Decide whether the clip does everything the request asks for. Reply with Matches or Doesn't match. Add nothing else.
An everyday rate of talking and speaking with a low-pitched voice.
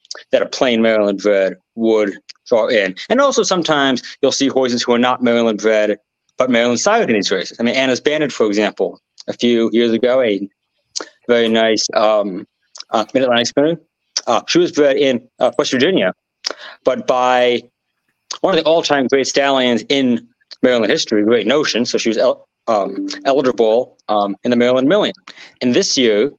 Matches